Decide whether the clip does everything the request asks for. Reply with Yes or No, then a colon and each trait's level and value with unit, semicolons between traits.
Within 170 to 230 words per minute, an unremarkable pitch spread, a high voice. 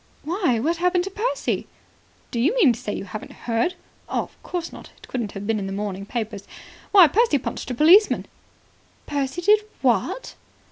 No: average, 180 wpm; wide, 8.3 semitones; very high, 280 Hz